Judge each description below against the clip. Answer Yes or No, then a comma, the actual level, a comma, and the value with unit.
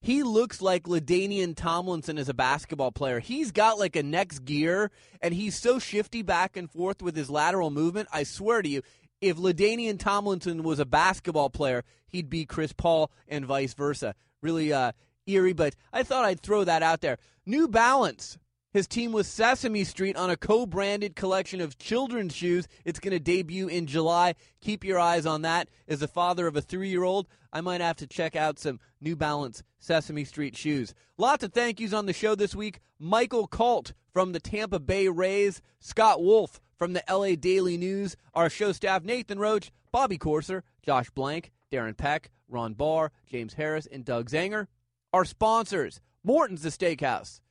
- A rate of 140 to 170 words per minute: No, average, 185 wpm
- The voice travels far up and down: No, average, 4.8 semitones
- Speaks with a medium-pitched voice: Yes, medium, 175 Hz